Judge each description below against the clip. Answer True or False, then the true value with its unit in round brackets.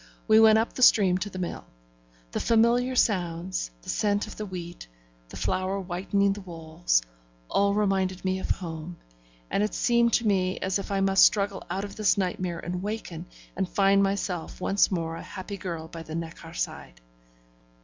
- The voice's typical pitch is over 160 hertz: True (190 Hz)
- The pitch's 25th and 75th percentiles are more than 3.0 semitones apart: False (2.7 semitones)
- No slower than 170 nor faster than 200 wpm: True (180 wpm)